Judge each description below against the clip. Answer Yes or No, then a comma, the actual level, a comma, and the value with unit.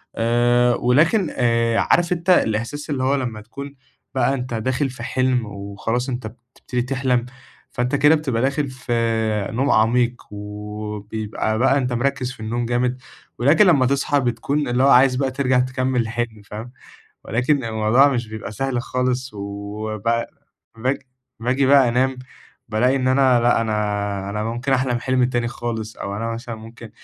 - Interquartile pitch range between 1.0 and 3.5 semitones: Yes, average, 2.7 semitones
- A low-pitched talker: Yes, low, 125 Hz